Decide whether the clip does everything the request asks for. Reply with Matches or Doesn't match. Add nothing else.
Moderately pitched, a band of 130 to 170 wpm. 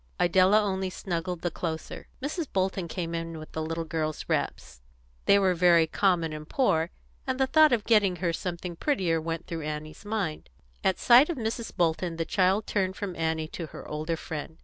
Doesn't match